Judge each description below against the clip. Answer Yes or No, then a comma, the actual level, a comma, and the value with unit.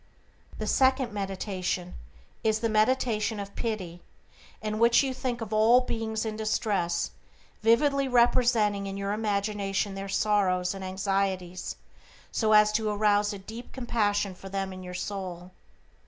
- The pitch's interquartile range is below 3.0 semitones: Yes, narrow, 2.5 semitones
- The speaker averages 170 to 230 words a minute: No, average, 140 wpm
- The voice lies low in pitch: No, high, 210 Hz